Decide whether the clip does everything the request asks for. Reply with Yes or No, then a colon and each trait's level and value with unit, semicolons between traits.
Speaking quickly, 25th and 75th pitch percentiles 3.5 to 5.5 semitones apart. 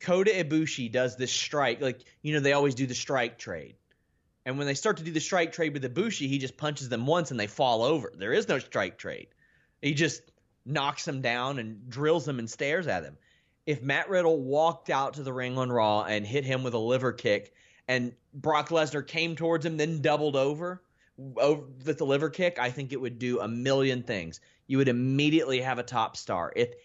Yes: fast, 220 wpm; average, 3.8 semitones